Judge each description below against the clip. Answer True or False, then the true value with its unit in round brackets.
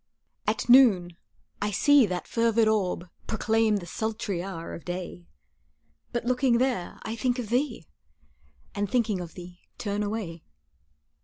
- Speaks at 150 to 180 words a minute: False (140 wpm)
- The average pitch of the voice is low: False (215 Hz)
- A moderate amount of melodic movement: True (4.8 semitones)